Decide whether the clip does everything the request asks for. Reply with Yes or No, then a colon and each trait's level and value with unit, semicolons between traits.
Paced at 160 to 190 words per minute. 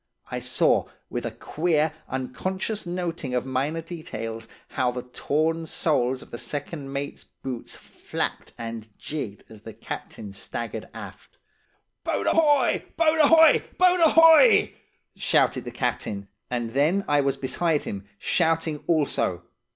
No: slow, 135 wpm